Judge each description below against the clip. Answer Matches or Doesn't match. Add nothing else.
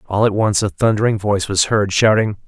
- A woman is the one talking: Doesn't match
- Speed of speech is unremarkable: Doesn't match